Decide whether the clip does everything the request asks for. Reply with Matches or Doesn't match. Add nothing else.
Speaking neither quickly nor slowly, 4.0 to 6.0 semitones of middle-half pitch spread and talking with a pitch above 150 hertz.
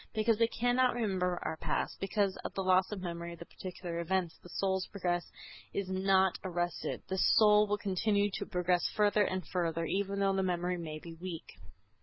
Doesn't match